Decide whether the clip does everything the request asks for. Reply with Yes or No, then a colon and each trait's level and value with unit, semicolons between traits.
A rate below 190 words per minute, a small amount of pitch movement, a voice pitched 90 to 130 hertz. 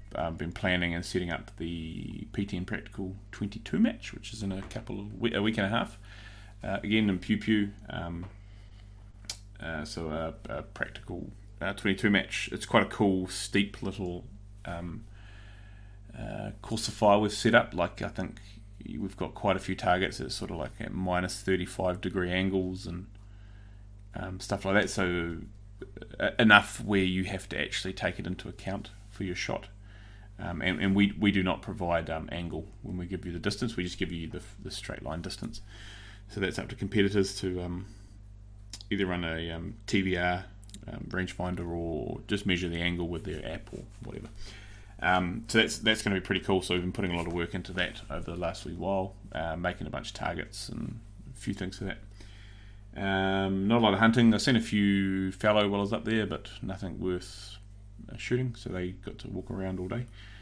No: average, 200 wpm; narrow, 2.1 semitones; low, 100 Hz